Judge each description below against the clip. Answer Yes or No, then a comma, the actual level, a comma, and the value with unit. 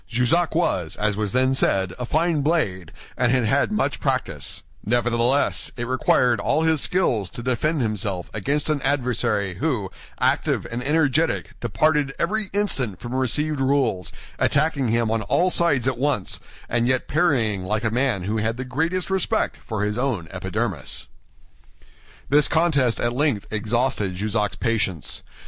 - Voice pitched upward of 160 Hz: No, low, 125 Hz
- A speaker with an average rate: Yes, average, 155 wpm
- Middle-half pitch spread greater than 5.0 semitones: Yes, wide, 5.4 semitones